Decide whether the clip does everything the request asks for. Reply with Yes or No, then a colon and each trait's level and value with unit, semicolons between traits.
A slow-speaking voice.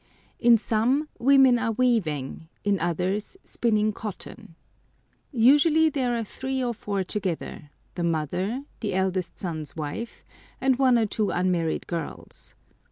Yes: slow, 125 wpm